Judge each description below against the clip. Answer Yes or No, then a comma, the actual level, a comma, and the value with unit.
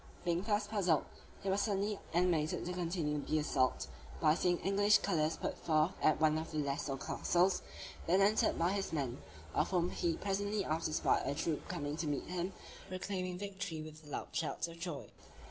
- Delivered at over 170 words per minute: Yes, average, 185 wpm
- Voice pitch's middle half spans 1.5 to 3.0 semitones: No, average, 3.8 semitones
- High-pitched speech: No, medium, 170 Hz